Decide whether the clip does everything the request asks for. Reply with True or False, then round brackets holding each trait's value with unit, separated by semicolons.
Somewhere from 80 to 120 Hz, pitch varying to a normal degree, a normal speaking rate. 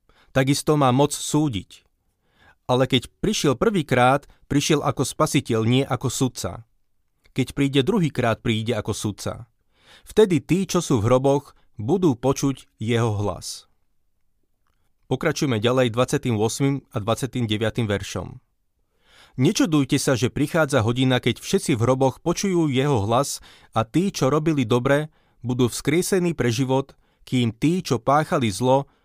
False (130 Hz; 4.0 semitones; 130 wpm)